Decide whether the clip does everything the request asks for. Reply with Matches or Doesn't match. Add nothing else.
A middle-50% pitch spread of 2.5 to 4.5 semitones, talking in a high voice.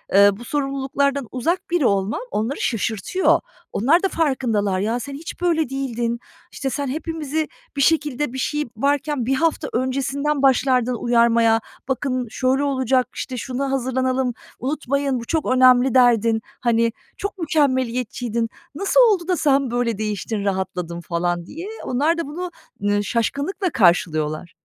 Matches